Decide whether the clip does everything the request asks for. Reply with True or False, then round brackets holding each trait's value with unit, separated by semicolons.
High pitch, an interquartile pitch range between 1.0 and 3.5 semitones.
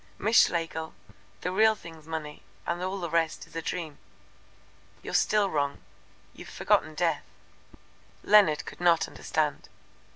False (165 Hz; 2.9 semitones)